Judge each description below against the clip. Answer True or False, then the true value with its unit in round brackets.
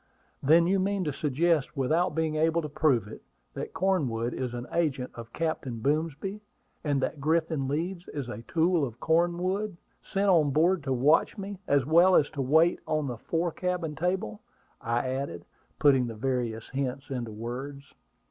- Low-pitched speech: False (150 Hz)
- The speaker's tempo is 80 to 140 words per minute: False (170 wpm)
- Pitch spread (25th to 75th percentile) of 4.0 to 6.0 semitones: True (4.7 semitones)